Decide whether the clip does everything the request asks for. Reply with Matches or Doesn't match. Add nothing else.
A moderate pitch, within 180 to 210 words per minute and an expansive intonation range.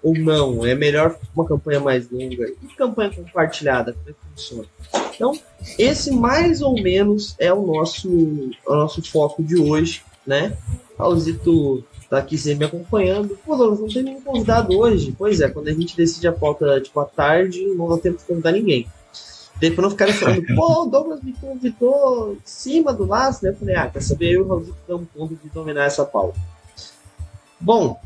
Matches